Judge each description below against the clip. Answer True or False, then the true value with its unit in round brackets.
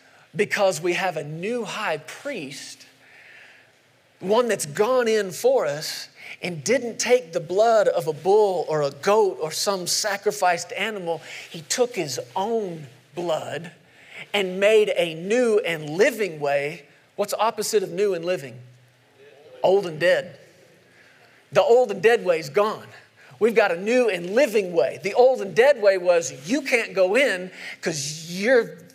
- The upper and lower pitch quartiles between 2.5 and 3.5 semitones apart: False (5.6 semitones)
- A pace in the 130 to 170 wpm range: True (155 wpm)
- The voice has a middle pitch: False (195 Hz)